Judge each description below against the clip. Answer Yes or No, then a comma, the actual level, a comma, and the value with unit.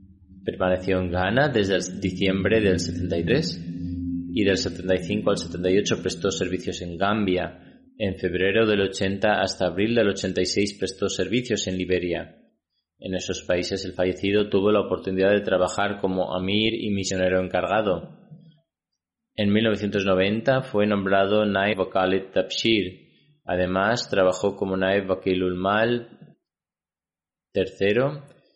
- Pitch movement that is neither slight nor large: No, narrow, 2.0 semitones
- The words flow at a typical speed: No, slow, 120 wpm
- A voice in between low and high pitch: No, very low, 95 Hz